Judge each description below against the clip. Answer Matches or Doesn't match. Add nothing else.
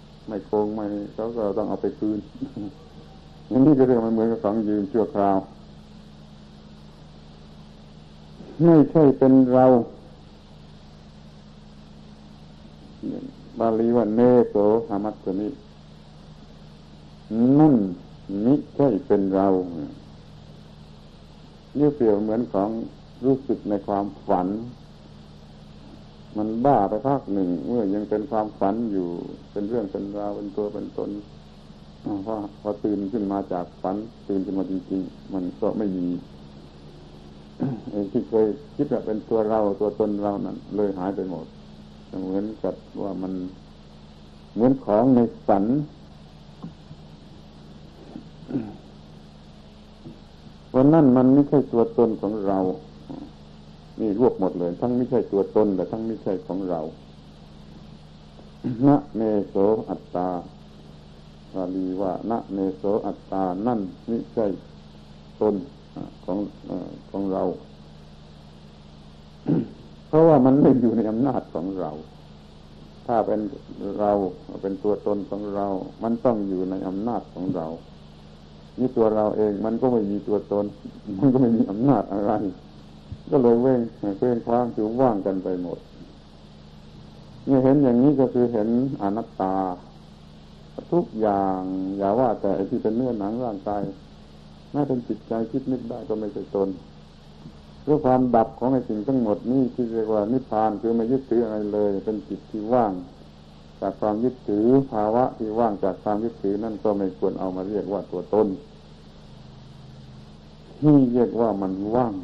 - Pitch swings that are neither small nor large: Doesn't match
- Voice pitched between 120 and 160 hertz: Doesn't match